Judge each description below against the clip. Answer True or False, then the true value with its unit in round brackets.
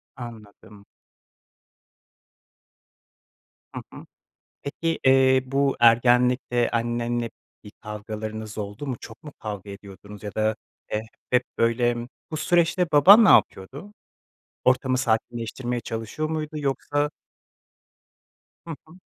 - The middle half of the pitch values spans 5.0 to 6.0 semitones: False (4.1 semitones)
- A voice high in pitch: False (120 Hz)